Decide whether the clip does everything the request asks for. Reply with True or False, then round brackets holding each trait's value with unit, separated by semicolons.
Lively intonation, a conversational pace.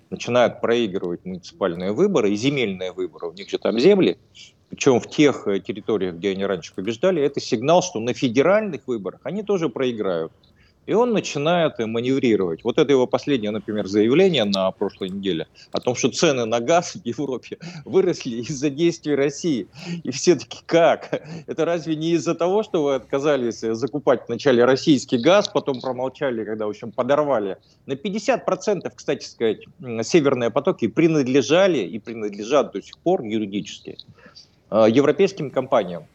True (6.2 semitones; 150 wpm)